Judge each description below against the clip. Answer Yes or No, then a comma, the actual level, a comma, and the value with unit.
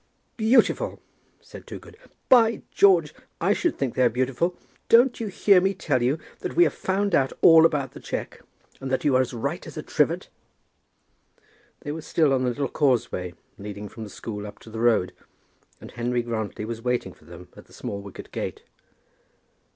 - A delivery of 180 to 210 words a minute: Yes, average, 185 wpm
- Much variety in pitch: Yes, wide, 7.1 semitones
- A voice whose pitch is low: Yes, low, 130 Hz